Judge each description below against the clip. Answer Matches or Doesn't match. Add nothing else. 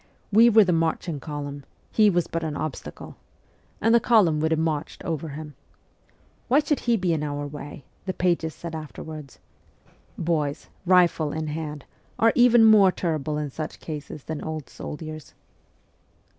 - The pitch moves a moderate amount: Matches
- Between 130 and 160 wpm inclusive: Doesn't match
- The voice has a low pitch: Doesn't match